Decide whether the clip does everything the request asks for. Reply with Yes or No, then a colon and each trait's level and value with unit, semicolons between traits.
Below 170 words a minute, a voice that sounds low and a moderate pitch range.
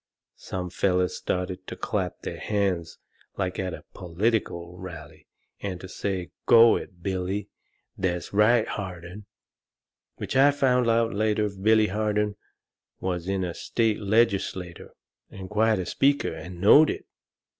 Yes: slow, 135 wpm; very low, 95 Hz; average, 3.2 semitones